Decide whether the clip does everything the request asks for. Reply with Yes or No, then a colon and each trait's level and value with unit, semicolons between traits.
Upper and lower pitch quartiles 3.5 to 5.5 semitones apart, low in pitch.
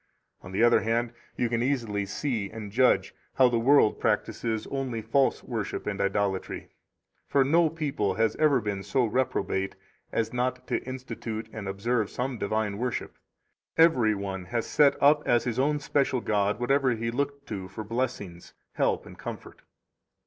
Yes: average, 4.0 semitones; low, 115 Hz